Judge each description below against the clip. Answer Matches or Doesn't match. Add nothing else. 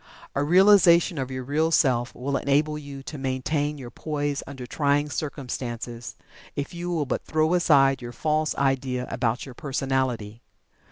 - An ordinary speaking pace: Matches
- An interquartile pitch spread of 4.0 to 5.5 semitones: Doesn't match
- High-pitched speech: Doesn't match